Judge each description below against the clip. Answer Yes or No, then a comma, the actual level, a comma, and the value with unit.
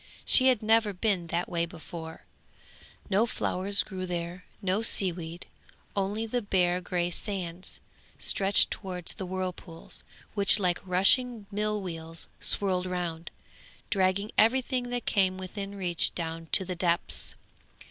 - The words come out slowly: Yes, slow, 130 wpm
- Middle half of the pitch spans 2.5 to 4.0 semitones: Yes, average, 2.8 semitones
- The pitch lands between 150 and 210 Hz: Yes, medium, 185 Hz